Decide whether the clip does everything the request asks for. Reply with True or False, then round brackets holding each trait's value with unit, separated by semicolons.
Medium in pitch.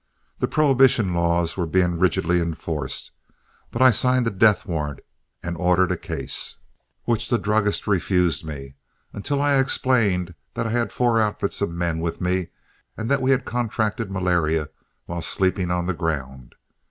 False (90 Hz)